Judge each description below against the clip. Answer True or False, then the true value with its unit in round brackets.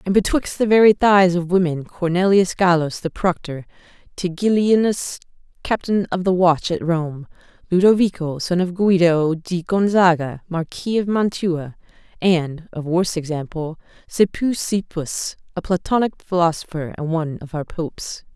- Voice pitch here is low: False (175 Hz)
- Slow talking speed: True (130 wpm)